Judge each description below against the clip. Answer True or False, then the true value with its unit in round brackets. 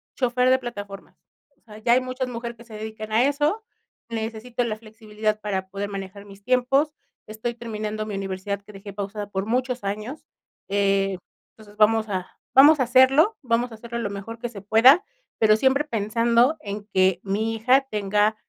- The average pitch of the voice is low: False (220 Hz)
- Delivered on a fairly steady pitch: False (3.3 semitones)